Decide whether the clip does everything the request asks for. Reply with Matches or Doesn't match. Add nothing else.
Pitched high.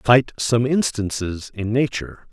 Doesn't match